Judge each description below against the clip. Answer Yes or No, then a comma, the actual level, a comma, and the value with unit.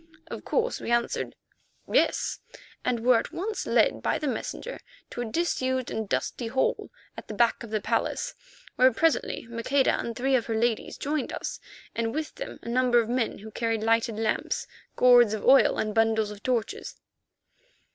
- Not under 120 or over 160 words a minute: No, average, 175 wpm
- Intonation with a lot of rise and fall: No, narrow, 2.5 semitones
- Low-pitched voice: No, high, 235 Hz